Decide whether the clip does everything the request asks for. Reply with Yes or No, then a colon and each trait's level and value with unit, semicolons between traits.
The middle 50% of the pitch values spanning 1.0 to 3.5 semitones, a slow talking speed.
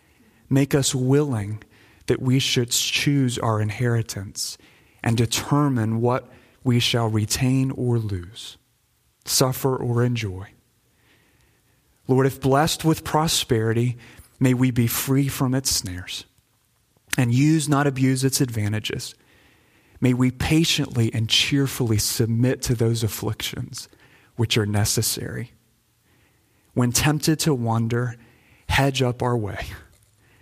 Yes: average, 3.0 semitones; slow, 115 wpm